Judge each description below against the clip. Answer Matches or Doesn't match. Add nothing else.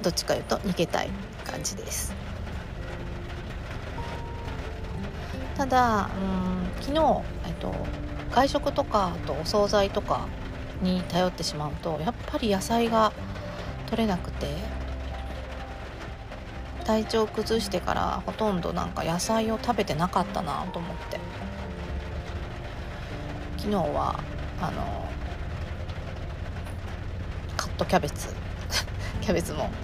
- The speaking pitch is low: Matches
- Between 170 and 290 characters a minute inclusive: Matches